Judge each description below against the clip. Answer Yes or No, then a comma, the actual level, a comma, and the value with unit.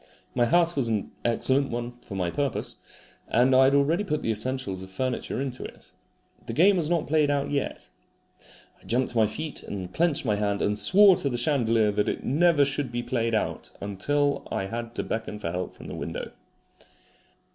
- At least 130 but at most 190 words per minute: No, average, 200 wpm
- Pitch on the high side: No, low, 125 Hz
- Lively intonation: No, average, 5.0 semitones